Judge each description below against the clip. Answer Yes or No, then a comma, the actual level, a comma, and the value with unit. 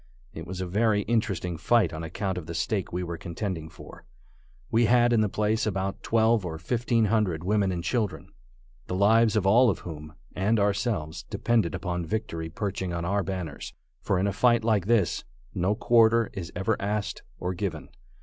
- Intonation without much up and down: No, average, 4.1 semitones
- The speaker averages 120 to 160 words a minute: No, average, 190 wpm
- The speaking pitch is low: Yes, low, 100 Hz